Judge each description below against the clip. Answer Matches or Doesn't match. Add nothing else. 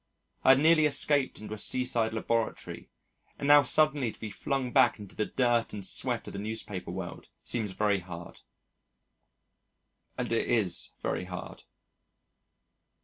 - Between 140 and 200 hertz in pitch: Doesn't match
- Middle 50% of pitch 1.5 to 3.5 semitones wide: Doesn't match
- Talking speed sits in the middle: Matches